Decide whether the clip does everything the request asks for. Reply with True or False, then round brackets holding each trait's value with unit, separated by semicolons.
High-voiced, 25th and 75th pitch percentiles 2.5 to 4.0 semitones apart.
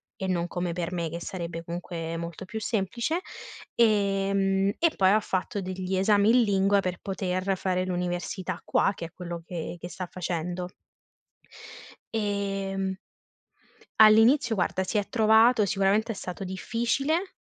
True (195 Hz; 2.9 semitones)